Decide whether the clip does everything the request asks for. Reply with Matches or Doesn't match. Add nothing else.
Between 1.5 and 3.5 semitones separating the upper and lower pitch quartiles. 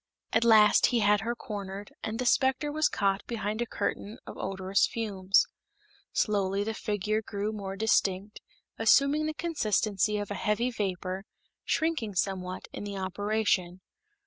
Matches